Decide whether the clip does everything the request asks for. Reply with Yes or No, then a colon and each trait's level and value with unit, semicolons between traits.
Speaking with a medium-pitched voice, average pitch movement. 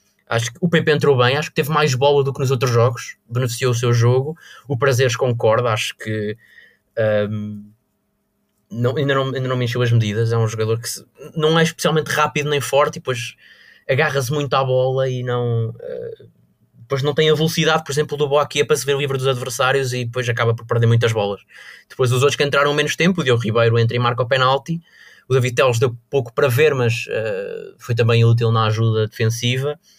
No: low, 130 Hz; average, 3.8 semitones